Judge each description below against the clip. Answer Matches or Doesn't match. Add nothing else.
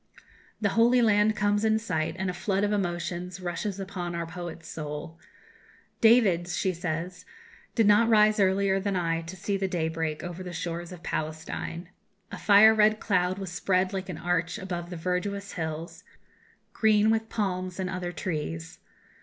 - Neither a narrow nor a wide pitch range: Matches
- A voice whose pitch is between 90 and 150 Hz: Doesn't match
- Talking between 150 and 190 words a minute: Matches